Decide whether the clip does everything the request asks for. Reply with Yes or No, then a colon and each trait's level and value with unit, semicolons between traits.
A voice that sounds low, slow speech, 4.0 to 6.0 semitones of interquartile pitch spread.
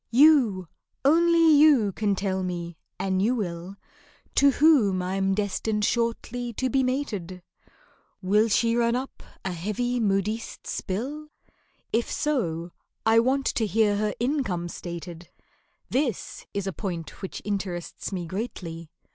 No: high, 210 Hz; slow, 125 wpm; average, 4.9 semitones